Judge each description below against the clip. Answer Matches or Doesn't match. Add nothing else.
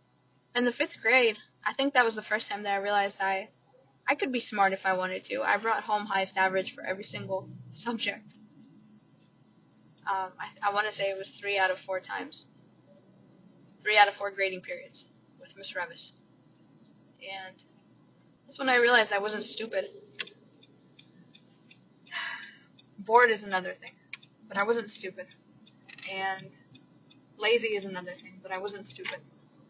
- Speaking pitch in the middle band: Doesn't match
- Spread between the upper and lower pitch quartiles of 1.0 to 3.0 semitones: Matches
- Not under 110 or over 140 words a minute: Doesn't match